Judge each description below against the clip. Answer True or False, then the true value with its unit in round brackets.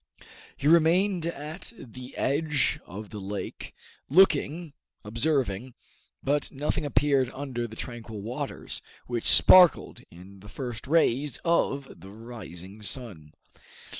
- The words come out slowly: True (115 wpm)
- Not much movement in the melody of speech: False (5.5 semitones)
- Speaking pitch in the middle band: False (130 Hz)